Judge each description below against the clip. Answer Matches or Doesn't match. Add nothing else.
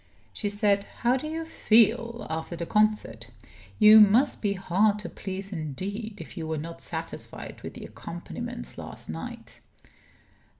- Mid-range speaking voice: Doesn't match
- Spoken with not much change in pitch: Doesn't match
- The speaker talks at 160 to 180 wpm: Doesn't match